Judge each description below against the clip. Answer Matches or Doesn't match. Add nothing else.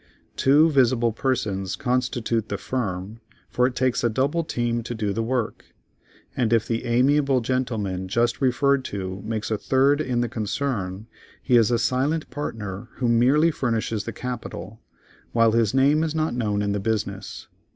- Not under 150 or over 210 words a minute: Matches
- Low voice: Matches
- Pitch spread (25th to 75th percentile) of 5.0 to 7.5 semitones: Doesn't match